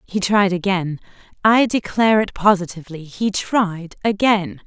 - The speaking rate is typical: No, slow, 115 wpm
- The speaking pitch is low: No, high, 195 Hz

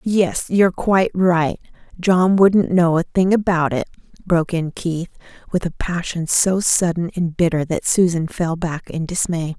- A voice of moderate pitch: Yes, medium, 175 Hz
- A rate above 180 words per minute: No, average, 165 wpm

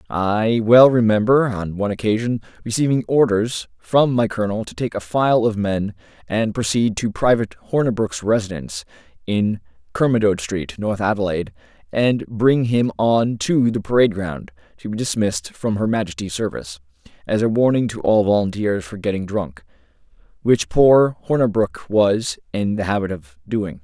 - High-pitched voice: No, low, 105 Hz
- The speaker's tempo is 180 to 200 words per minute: No, average, 155 wpm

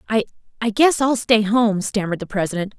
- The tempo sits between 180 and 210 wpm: No, average, 170 wpm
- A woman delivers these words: Yes, female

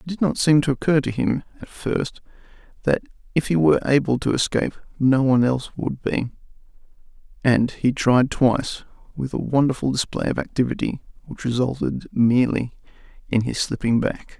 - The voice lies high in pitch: No, low, 135 Hz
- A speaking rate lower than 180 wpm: Yes, average, 165 wpm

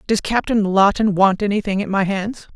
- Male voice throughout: No, female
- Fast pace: No, average, 190 wpm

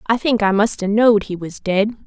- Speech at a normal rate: No, fast, 260 wpm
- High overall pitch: Yes, high, 210 Hz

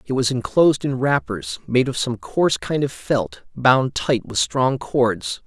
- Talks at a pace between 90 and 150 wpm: No, average, 185 wpm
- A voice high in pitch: No, low, 130 Hz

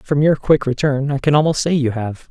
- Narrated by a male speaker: Yes, male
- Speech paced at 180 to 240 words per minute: No, fast, 260 wpm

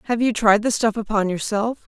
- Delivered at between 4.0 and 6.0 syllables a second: Yes, 5.6 syllables/s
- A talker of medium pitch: No, high, 220 Hz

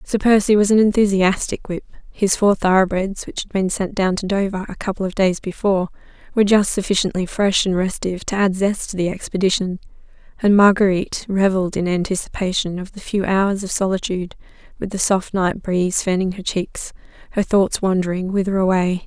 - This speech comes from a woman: Yes, female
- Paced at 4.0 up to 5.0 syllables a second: No, 5.7 syllables/s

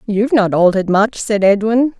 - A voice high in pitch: Yes, high, 215 Hz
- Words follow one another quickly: No, average, 180 wpm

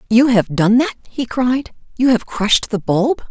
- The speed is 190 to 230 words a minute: Yes, average, 200 wpm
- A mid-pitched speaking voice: No, high, 240 Hz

